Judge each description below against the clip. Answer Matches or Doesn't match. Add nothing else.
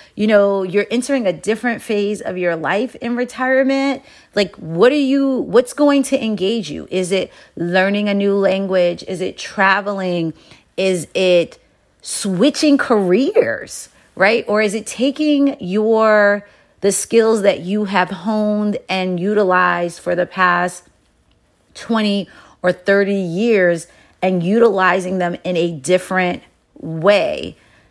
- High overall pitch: Matches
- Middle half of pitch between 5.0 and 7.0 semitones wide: Doesn't match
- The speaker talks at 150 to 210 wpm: Doesn't match